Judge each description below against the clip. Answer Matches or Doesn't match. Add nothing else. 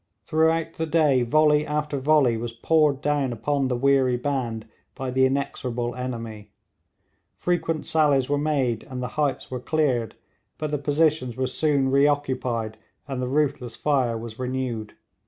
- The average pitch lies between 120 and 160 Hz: Matches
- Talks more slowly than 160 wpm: Matches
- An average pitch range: Matches